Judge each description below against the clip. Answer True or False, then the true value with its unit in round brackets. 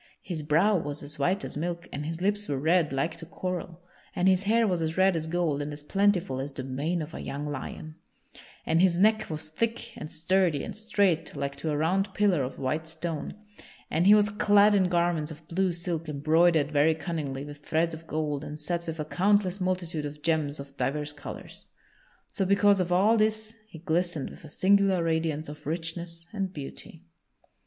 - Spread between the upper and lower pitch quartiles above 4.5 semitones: False (3.7 semitones)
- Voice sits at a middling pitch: True (165 Hz)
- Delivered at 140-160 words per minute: False (200 wpm)